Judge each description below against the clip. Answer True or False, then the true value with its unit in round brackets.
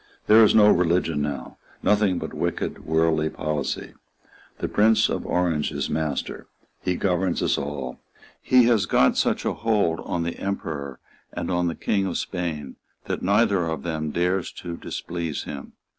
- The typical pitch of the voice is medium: False (85 Hz)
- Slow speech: False (160 wpm)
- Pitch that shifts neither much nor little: True (3.9 semitones)